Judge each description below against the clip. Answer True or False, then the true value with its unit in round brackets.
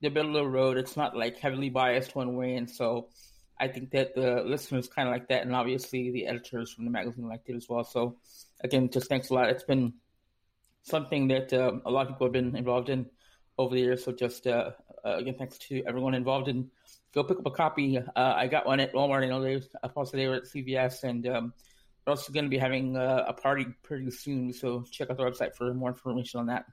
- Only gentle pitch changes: True (1.3 semitones)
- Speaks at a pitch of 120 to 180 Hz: True (130 Hz)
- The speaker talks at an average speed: False (240 wpm)